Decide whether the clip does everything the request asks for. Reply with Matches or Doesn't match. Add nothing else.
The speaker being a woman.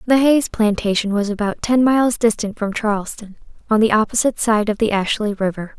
Matches